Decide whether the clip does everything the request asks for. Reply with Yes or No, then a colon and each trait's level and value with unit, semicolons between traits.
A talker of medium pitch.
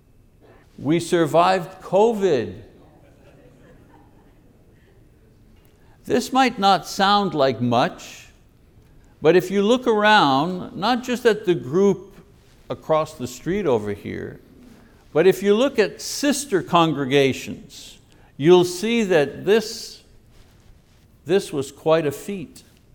Yes: medium, 180 Hz